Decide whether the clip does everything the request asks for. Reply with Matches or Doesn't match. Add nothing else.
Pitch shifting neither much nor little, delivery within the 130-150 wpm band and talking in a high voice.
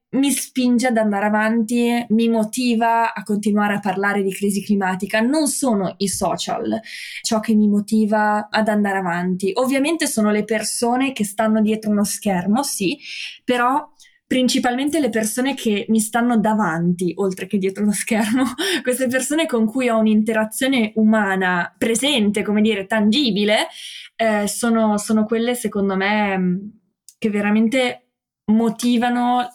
Matches